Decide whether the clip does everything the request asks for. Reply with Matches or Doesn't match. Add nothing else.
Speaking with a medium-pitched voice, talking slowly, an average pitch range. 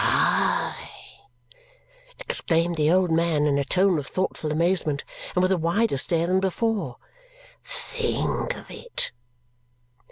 Matches